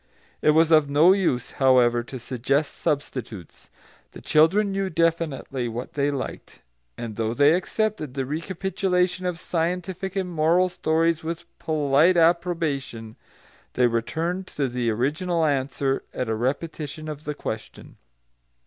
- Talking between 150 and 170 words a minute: No, slow, 135 wpm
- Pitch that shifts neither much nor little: Yes, average, 4.7 semitones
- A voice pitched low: No, medium, 155 Hz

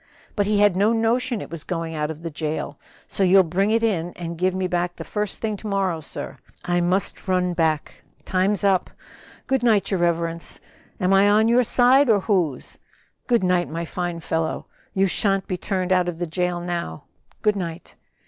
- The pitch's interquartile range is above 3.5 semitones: No, average, 3.2 semitones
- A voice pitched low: No, medium, 185 Hz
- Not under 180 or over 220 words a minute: Yes, average, 200 wpm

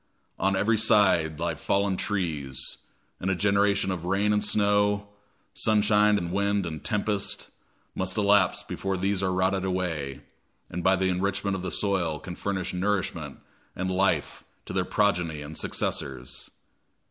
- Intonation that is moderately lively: No, narrow, 2.2 semitones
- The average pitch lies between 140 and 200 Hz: No, very low, 95 Hz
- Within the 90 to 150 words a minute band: Yes, average, 145 wpm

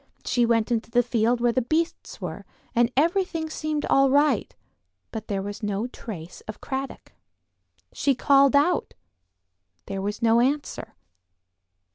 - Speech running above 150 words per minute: No, average, 140 wpm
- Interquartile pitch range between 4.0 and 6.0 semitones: Yes, average, 4.3 semitones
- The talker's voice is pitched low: No, high, 245 Hz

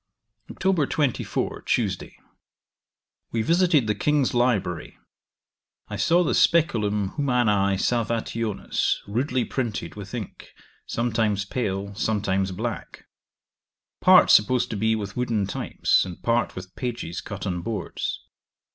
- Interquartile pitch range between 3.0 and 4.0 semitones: Yes, average, 3.6 semitones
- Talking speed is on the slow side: Yes, slow, 115 wpm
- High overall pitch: No, low, 110 Hz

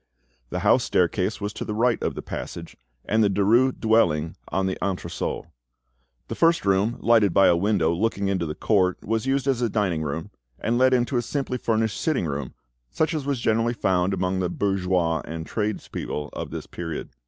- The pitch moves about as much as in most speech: Yes, average, 4.7 semitones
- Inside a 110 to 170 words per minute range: No, average, 190 wpm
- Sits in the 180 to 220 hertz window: No, low, 100 Hz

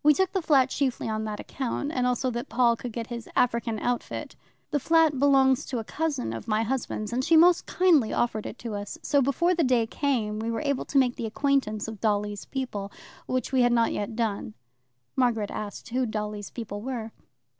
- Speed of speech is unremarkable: No, fast, 210 wpm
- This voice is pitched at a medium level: No, high, 245 Hz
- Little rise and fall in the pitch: No, average, 4.0 semitones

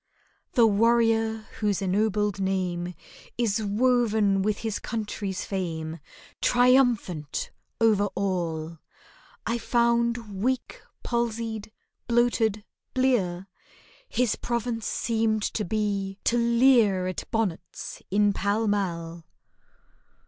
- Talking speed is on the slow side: Yes, slow, 95 wpm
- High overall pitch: Yes, high, 215 Hz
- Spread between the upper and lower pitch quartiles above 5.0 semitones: No, average, 3.3 semitones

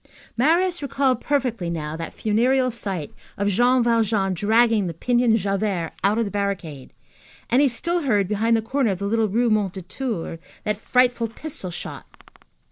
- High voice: Yes, high, 220 Hz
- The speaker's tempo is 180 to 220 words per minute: No, average, 160 wpm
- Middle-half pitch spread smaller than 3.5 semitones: No, average, 4.1 semitones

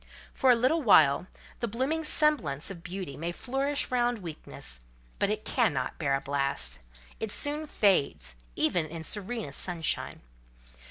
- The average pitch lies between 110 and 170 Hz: No, high, 190 Hz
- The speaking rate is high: No, average, 145 wpm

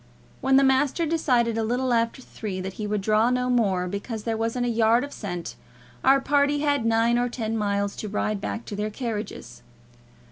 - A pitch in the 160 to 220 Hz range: No, high, 230 Hz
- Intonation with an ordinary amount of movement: Yes, average, 3.2 semitones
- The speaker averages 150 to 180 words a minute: No, average, 200 wpm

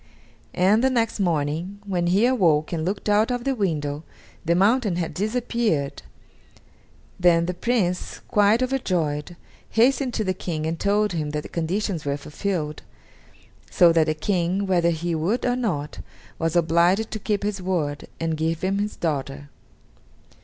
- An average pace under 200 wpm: Yes, average, 160 wpm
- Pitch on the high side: No, medium, 180 Hz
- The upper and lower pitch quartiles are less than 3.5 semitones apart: No, average, 4.6 semitones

